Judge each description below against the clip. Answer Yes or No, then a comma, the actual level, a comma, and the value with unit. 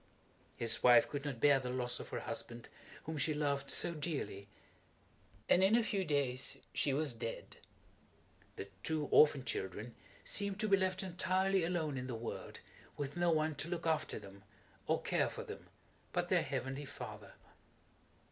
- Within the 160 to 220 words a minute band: Yes, average, 165 wpm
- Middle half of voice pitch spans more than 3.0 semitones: Yes, wide, 5.6 semitones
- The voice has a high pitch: No, medium, 145 Hz